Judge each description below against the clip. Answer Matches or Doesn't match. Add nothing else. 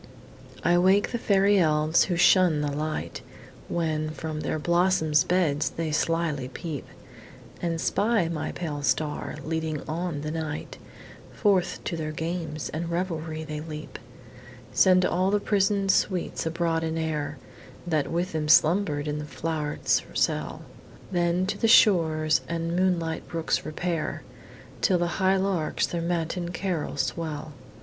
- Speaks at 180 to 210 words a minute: Doesn't match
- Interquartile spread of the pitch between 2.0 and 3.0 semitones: Matches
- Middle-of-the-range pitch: Matches